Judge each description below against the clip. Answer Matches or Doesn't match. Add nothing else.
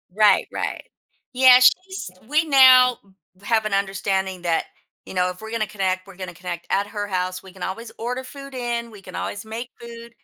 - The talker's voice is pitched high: Matches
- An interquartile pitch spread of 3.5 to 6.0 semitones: Matches